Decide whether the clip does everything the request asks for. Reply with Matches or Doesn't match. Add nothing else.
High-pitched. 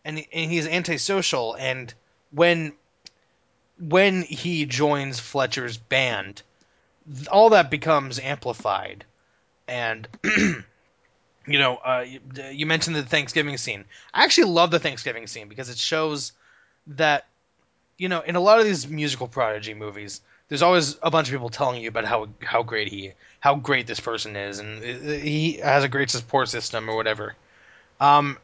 Doesn't match